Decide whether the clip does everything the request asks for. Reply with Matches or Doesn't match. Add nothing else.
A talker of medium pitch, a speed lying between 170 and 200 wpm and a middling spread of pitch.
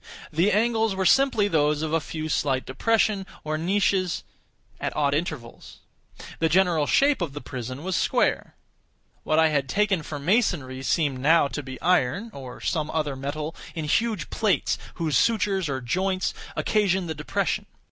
Doesn't match